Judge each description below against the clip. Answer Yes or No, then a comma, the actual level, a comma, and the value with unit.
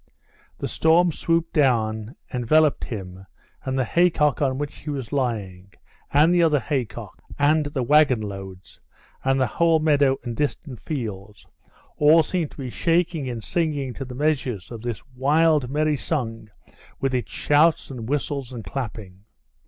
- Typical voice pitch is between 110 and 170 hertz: Yes, low, 135 Hz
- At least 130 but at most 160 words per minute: Yes, average, 155 wpm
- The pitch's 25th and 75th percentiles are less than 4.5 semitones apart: No, average, 4.8 semitones